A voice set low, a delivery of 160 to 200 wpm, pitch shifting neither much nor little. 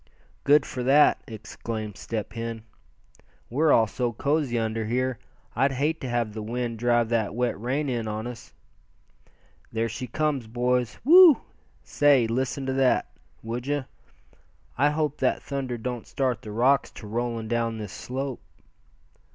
No: low, 120 Hz; average, 150 wpm; average, 3.0 semitones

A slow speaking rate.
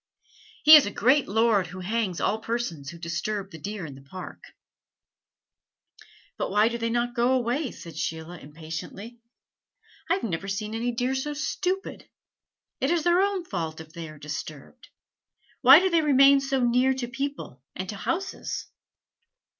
No: average, 165 wpm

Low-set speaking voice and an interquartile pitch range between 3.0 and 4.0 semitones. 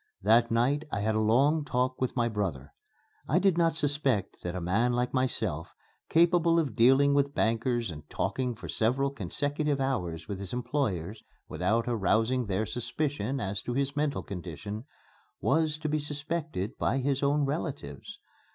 No: low, 125 Hz; average, 5.1 semitones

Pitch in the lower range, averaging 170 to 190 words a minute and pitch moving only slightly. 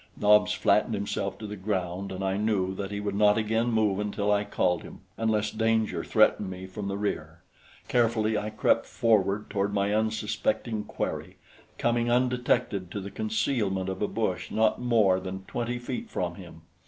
Yes: low, 105 Hz; average, 175 wpm; narrow, 2.2 semitones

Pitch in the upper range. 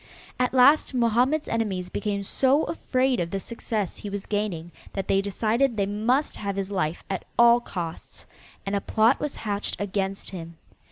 Yes: high, 205 Hz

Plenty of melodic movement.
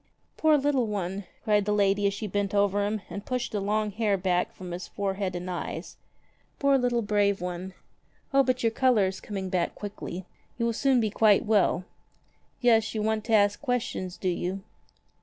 No: average, 2.9 semitones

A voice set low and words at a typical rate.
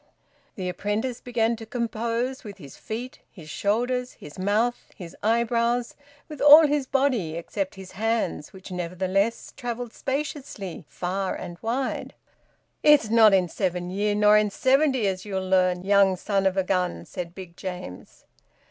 No: high, 210 Hz; average, 150 wpm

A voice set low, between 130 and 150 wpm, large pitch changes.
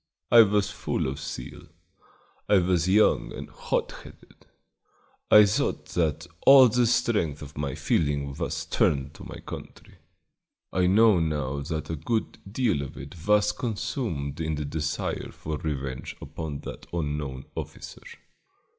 Yes: very low, 80 Hz; average, 145 wpm; wide, 6.4 semitones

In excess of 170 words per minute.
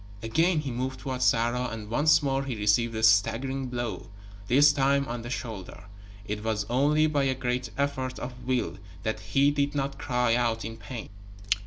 Yes: average, 180 wpm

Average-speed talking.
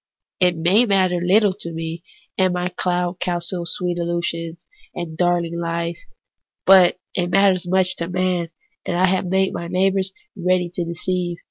Yes: average, 160 wpm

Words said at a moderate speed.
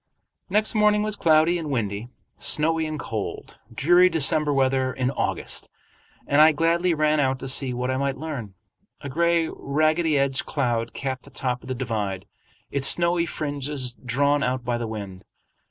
Yes: average, 170 wpm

